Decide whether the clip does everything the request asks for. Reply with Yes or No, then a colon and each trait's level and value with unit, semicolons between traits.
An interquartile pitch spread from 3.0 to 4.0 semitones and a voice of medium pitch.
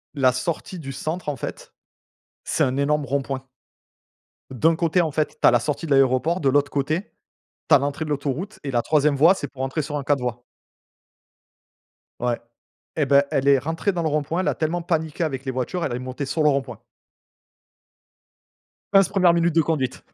Yes: average, 3.3 semitones; medium, 145 Hz